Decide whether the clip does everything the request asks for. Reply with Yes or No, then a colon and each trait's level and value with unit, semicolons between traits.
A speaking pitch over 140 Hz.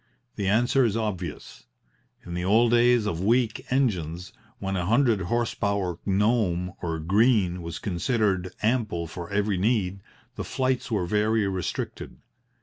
No: low, 100 Hz